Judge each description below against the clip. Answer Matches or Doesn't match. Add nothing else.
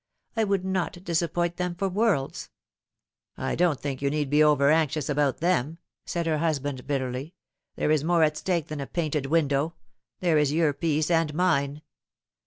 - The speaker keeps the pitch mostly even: Doesn't match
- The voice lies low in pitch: Doesn't match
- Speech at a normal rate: Matches